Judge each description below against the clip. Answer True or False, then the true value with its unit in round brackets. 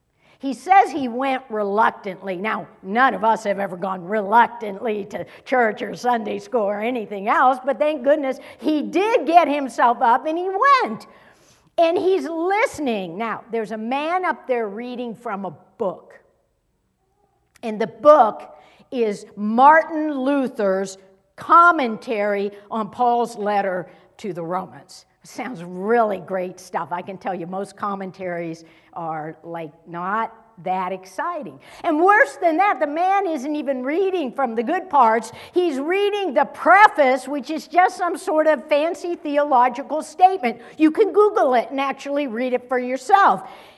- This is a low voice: False (245 Hz)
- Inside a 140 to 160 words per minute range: True (150 wpm)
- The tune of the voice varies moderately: False (7.1 semitones)